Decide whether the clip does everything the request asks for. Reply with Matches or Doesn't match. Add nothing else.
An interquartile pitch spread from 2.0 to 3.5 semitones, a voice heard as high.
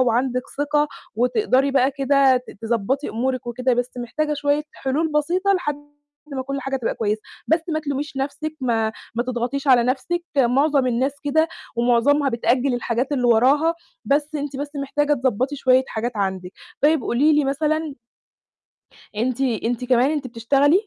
Matches